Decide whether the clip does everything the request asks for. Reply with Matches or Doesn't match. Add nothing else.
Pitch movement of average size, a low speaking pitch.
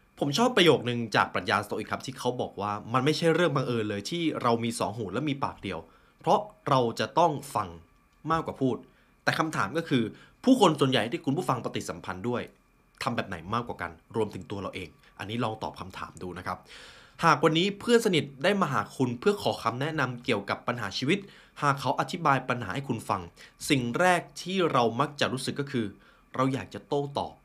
Doesn't match